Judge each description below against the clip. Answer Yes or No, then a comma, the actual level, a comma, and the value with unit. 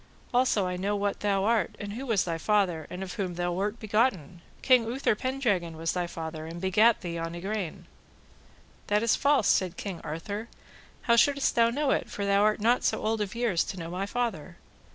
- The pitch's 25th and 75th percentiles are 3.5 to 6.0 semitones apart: Yes, average, 4.7 semitones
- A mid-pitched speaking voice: No, high, 200 Hz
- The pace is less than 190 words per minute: No, fast, 205 wpm